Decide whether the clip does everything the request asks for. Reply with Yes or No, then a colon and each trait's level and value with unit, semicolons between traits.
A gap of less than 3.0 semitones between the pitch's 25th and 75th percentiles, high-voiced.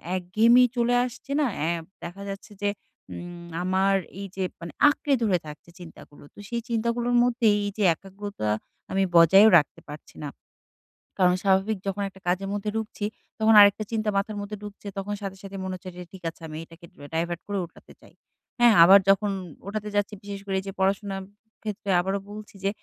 Yes: narrow, 2.5 semitones; high, 195 Hz